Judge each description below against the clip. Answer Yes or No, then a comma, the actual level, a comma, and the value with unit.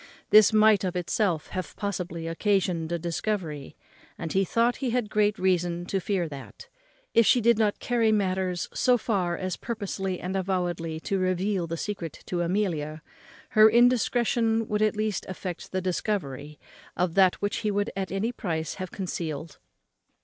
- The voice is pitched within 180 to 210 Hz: Yes, high, 190 Hz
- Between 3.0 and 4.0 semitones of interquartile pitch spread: Yes, average, 3.6 semitones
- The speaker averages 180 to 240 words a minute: No, average, 165 wpm